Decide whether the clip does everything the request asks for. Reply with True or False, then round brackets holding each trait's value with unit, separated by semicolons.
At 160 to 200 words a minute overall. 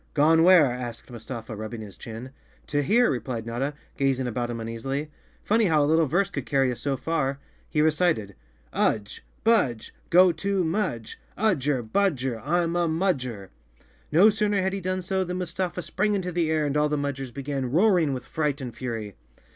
True (185 wpm)